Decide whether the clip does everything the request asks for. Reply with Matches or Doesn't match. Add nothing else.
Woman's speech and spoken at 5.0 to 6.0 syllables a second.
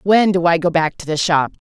Matches